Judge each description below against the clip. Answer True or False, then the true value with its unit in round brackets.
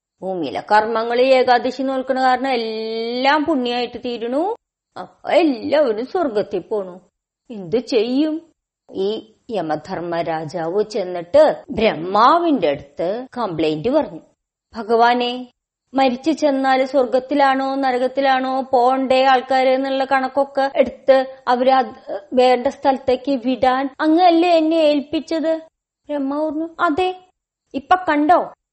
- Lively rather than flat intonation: False (3.7 semitones)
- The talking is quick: False (90 wpm)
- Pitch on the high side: True (265 Hz)